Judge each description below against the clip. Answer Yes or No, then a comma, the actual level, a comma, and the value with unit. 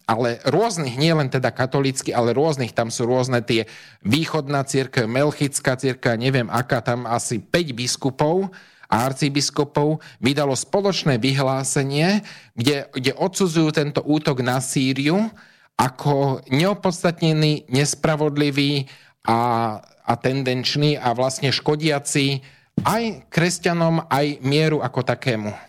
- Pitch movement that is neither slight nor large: Yes, average, 3.2 semitones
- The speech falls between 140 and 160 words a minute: No, slow, 110 wpm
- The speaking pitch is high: No, medium, 140 Hz